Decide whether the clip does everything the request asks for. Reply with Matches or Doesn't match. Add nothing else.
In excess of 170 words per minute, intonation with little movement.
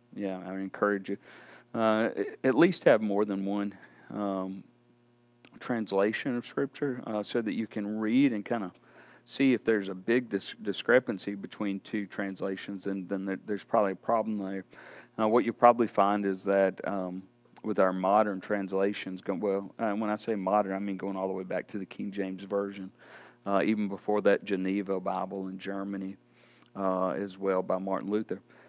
Matches